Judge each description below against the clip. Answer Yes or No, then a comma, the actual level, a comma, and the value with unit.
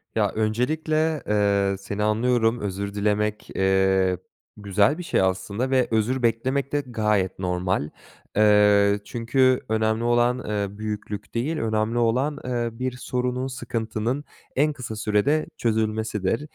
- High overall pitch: No, low, 110 Hz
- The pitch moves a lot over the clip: No, average, 3.5 semitones